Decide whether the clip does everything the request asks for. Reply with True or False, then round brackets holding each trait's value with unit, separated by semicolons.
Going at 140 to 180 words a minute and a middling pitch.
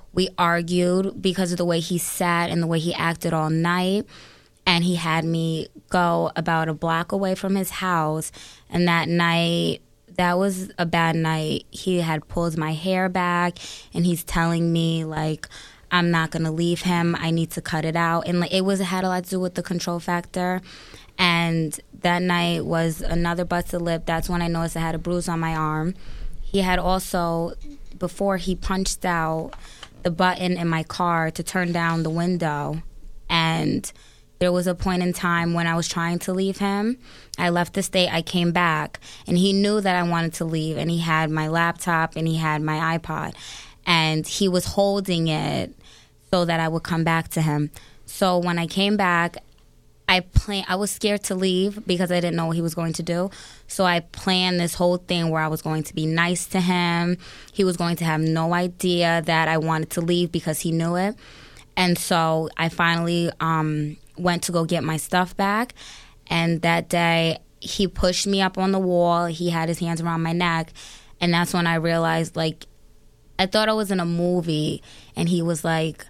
False (205 wpm; 170 Hz)